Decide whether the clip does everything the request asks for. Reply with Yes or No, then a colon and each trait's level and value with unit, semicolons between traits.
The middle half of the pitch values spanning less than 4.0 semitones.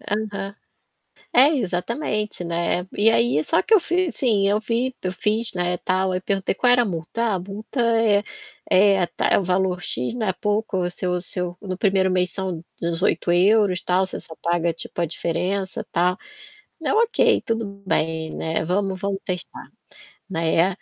Yes: average, 3.1 semitones